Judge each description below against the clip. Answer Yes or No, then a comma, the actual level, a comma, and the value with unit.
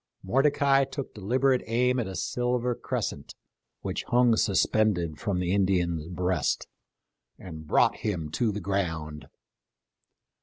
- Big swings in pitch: Yes, wide, 5.8 semitones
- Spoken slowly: Yes, slow, 120 wpm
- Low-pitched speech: Yes, low, 100 Hz